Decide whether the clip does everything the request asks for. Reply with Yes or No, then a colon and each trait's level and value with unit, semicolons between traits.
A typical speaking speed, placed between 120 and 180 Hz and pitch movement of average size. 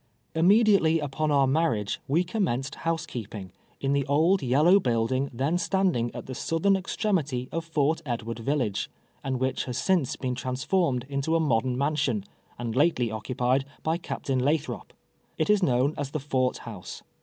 Yes: average, 165 wpm; medium, 140 Hz; average, 4.7 semitones